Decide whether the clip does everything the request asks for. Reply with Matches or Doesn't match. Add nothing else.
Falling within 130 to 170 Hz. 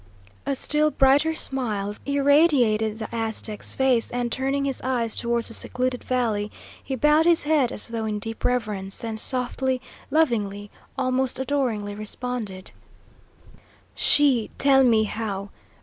Doesn't match